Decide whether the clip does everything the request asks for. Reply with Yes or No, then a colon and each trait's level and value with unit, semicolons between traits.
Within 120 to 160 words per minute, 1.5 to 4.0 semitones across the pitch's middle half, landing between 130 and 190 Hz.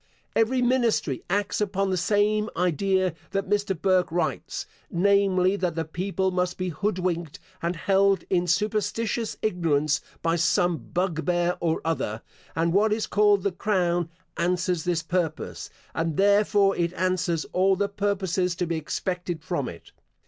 Yes: average, 150 wpm; average, 2.8 semitones; medium, 185 Hz